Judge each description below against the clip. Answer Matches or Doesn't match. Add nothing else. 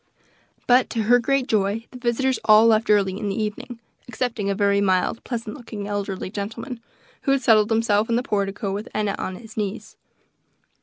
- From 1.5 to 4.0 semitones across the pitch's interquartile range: Matches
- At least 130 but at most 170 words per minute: Doesn't match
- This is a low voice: Doesn't match